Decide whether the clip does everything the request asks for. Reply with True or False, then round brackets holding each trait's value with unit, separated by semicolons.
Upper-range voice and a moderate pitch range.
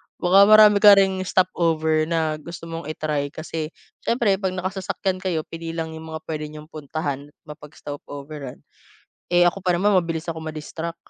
False (165 Hz; 3.1 semitones)